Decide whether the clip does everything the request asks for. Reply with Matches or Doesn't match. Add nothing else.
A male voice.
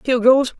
Matches